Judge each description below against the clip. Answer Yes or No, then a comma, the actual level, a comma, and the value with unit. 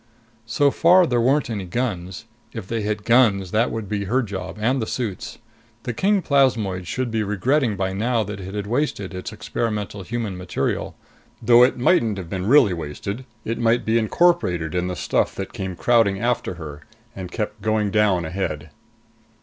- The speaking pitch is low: Yes, low, 105 Hz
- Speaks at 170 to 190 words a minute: Yes, average, 180 wpm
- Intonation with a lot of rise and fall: No, average, 4.2 semitones